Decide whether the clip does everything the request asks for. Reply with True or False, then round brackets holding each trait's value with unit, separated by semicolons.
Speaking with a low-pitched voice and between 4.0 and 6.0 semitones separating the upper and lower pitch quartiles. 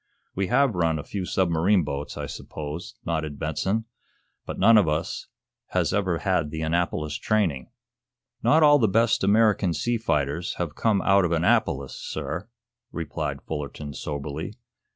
True (85 Hz; 5.3 semitones)